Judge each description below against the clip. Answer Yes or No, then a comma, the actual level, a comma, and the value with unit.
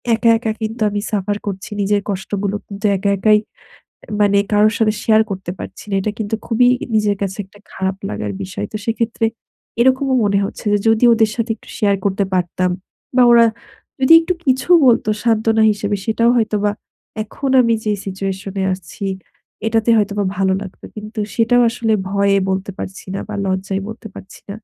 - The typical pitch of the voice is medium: No, high, 210 Hz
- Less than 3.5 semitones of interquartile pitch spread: Yes, narrow, 2.4 semitones